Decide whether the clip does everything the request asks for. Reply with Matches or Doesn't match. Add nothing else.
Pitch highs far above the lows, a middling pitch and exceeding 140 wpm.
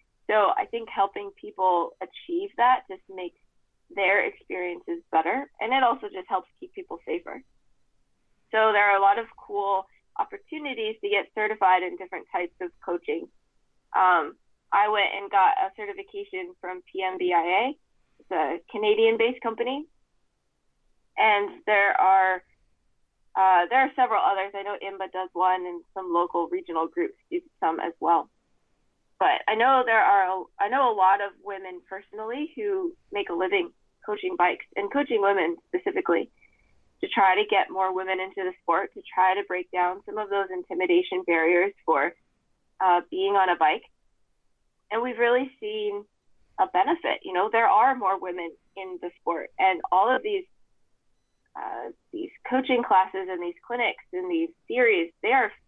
Doesn't match